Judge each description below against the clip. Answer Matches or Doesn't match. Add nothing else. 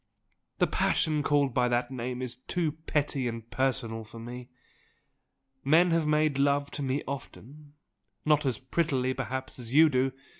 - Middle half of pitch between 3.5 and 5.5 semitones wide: Doesn't match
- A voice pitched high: Doesn't match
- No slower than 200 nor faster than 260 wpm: Doesn't match